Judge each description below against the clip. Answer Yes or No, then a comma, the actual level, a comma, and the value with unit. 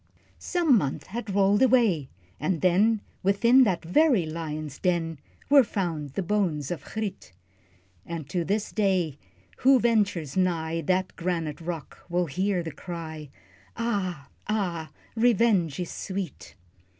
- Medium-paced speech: No, slow, 130 wpm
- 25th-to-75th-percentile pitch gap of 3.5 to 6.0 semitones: Yes, average, 4.4 semitones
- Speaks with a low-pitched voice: No, medium, 180 Hz